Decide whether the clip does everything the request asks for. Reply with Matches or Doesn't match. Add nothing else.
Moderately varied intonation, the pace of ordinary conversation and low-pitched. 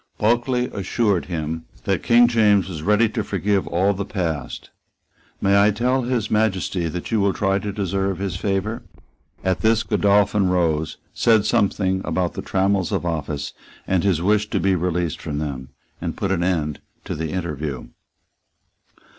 Matches